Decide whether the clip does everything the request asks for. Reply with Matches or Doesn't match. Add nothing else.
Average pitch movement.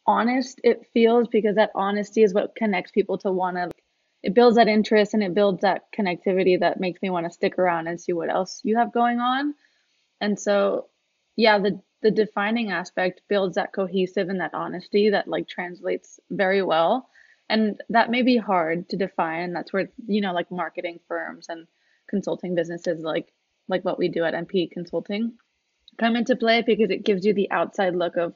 Matches